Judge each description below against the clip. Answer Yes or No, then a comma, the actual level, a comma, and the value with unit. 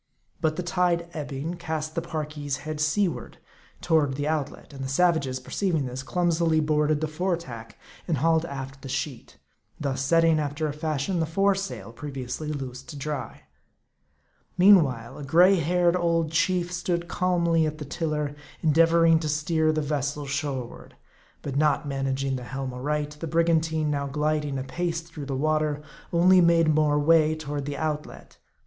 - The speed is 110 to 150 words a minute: No, average, 165 wpm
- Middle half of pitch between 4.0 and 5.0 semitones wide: No, average, 2.9 semitones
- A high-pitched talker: No, medium, 155 Hz